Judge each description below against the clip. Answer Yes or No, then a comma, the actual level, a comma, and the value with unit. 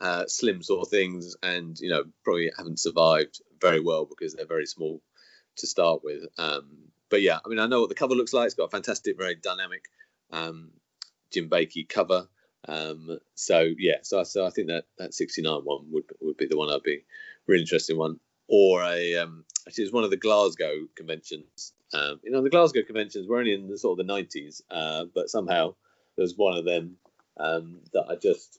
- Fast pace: Yes, fast, 210 wpm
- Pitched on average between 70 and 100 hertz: Yes, very low, 95 Hz